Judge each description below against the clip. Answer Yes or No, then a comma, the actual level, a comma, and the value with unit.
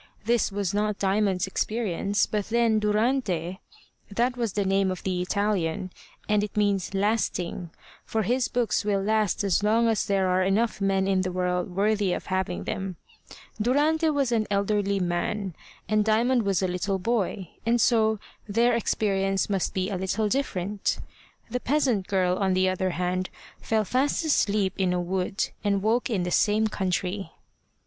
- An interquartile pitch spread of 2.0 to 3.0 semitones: Yes, average, 2.7 semitones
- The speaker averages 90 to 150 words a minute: No, average, 165 wpm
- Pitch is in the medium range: No, high, 200 Hz